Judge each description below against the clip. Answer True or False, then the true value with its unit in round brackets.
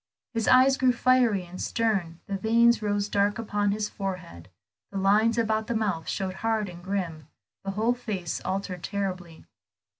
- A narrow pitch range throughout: False (3.2 semitones)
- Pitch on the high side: True (205 Hz)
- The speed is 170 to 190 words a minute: False (160 wpm)